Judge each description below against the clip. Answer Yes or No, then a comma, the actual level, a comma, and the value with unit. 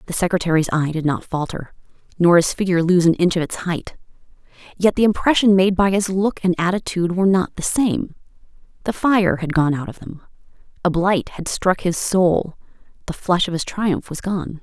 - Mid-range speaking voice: Yes, medium, 180 Hz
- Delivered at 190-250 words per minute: Yes, average, 195 wpm